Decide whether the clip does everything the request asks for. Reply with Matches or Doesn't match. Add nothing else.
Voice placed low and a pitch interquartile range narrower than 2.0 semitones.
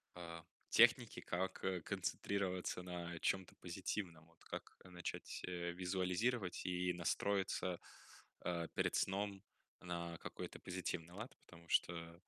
Matches